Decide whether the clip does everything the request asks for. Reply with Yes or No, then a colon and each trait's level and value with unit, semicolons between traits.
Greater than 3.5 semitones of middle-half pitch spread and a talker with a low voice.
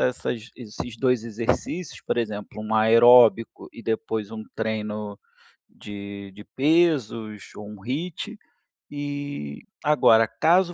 Yes: average, 5.1 semitones; low, 115 Hz